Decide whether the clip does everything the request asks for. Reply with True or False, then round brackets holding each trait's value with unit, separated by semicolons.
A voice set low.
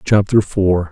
True (95 Hz)